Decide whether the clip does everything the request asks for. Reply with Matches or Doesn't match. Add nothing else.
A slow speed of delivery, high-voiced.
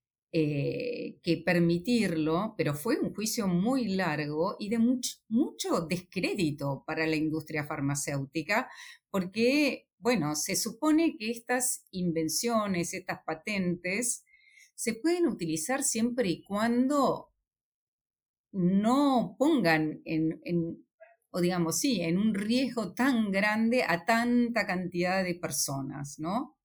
Matches